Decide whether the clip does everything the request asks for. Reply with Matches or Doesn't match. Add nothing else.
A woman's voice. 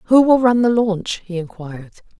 Matches